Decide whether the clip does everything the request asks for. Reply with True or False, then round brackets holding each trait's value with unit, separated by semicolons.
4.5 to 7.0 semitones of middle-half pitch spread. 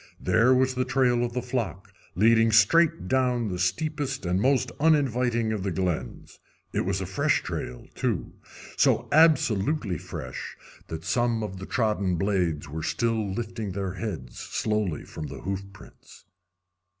True (5.2 semitones)